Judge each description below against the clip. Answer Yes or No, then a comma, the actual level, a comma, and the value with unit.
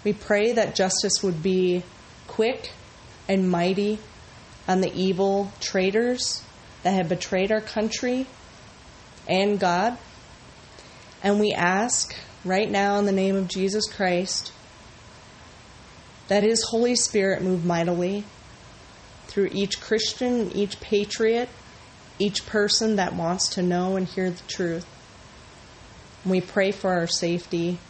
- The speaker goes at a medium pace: No, slow, 125 wpm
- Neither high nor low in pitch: No, high, 195 Hz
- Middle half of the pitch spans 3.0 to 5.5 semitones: No, narrow, 2.6 semitones